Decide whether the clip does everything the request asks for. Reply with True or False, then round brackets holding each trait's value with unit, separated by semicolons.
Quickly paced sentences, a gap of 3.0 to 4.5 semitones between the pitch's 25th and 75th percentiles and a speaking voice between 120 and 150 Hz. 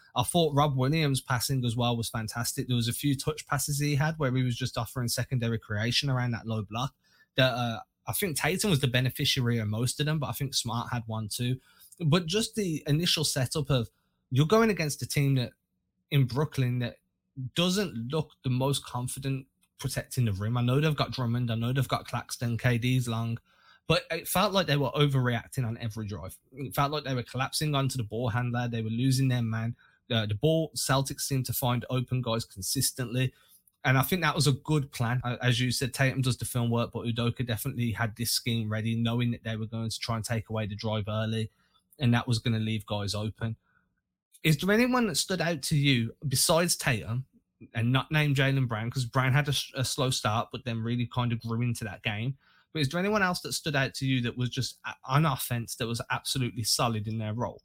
True (225 wpm; 3.3 semitones; 125 Hz)